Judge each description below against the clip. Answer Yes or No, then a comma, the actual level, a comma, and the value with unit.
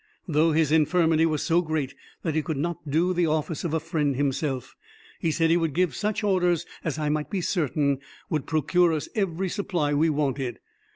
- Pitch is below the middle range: No, medium, 160 Hz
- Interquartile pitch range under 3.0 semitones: Yes, narrow, 2.6 semitones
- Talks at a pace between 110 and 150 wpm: No, average, 195 wpm